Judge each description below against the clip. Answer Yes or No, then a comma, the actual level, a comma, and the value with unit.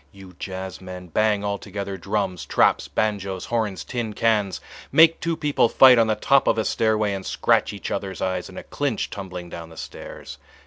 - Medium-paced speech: Yes, average, 175 wpm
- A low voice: Yes, low, 100 Hz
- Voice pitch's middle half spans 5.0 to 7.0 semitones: No, average, 2.8 semitones